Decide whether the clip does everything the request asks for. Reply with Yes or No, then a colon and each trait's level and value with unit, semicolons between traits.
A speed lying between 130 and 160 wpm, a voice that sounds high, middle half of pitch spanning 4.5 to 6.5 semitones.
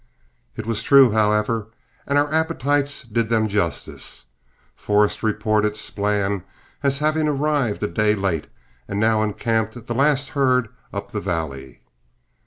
No: slow, 135 wpm; low, 110 Hz; average, 4.8 semitones